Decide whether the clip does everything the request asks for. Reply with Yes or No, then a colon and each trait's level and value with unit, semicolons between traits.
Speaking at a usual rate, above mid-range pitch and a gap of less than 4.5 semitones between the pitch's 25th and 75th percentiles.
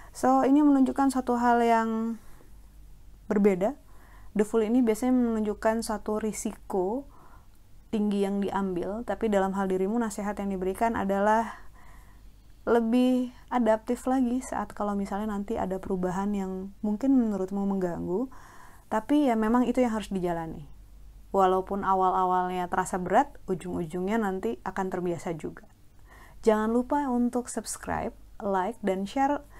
Yes: average, 125 wpm; high, 210 Hz; average, 3.7 semitones